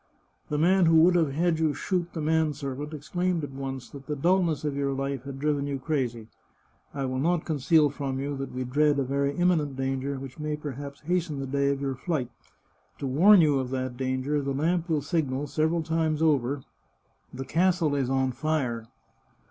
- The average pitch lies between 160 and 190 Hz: No, medium, 145 Hz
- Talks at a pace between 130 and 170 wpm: No, fast, 205 wpm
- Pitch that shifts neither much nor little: Yes, average, 3.0 semitones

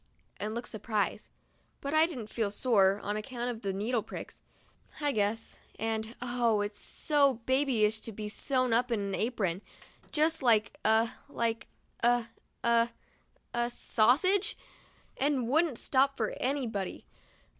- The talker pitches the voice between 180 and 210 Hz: No, high, 235 Hz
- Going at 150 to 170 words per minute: Yes, average, 165 wpm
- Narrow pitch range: No, average, 3.4 semitones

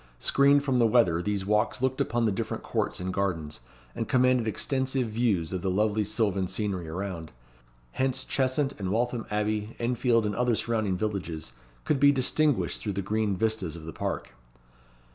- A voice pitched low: Yes, low, 110 Hz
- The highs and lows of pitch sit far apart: No, average, 4.6 semitones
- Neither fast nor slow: Yes, average, 170 wpm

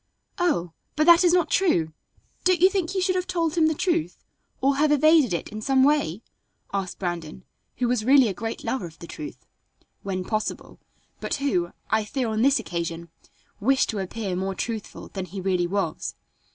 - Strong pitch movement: Yes, wide, 8.6 semitones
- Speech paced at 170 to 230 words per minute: Yes, average, 190 wpm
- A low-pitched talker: No, high, 230 Hz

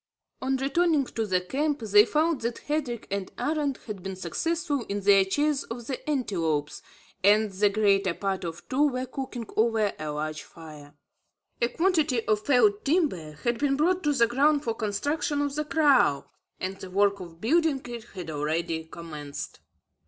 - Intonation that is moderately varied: No, wide, 7.4 semitones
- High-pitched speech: Yes, high, 230 Hz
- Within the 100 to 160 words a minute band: No, average, 170 wpm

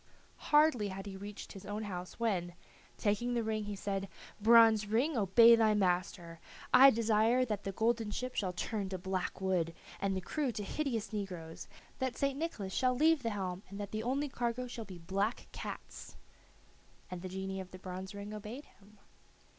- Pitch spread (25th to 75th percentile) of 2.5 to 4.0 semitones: Yes, average, 3.6 semitones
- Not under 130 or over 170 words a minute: No, average, 185 wpm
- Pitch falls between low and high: No, high, 210 Hz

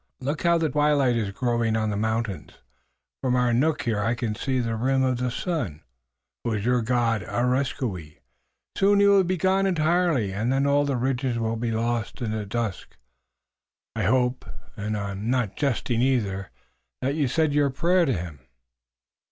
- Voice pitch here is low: Yes, low, 125 Hz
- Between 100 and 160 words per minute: No, average, 180 wpm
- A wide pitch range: No, average, 4.3 semitones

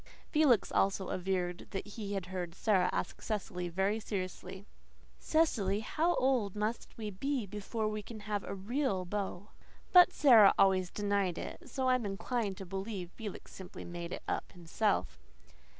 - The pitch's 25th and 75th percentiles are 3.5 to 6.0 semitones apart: No, average, 3.0 semitones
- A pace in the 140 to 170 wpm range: Yes, average, 155 wpm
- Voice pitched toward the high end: Yes, high, 200 Hz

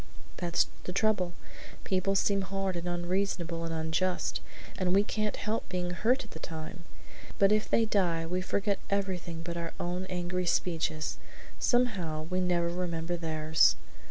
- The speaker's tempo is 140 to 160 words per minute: Yes, average, 155 wpm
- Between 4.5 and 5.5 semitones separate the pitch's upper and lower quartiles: No, narrow, 2.6 semitones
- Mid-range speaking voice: Yes, medium, 180 Hz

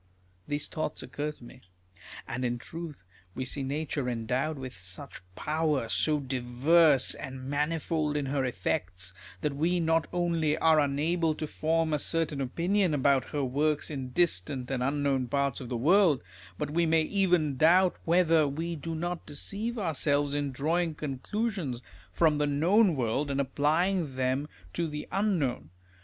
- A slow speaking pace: No, average, 160 wpm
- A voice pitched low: No, medium, 150 Hz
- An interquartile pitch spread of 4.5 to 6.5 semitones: No, average, 3.7 semitones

